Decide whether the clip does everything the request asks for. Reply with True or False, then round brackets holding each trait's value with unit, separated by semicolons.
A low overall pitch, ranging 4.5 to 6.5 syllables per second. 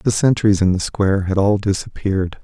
True (100 Hz; 5.4 syllables/s)